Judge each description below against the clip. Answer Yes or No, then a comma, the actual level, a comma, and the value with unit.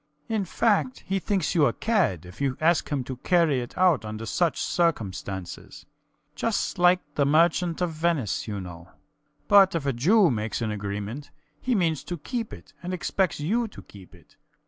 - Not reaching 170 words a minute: No, average, 180 wpm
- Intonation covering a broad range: Yes, wide, 8.5 semitones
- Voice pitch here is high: No, medium, 155 Hz